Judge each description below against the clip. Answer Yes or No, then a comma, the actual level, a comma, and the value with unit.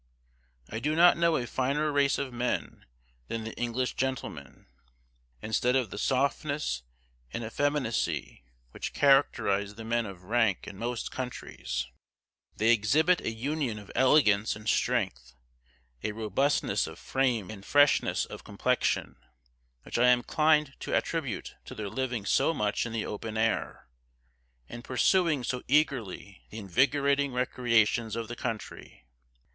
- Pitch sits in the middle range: No, low, 120 Hz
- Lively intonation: No, average, 4.5 semitones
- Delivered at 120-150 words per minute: Yes, average, 140 wpm